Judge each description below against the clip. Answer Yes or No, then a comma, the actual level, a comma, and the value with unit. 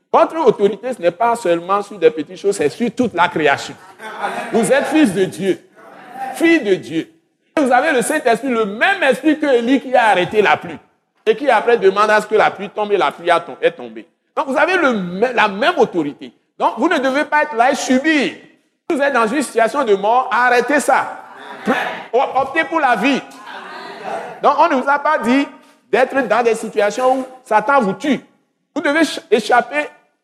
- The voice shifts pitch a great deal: Yes, wide, 5.7 semitones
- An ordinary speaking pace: Yes, average, 195 wpm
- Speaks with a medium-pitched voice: No, very high, 260 Hz